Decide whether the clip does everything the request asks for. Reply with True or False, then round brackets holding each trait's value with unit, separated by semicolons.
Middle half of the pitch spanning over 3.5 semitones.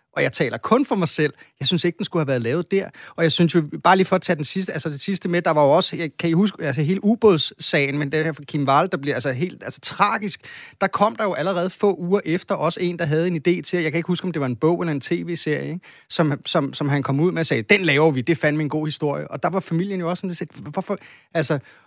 False (3.1 semitones)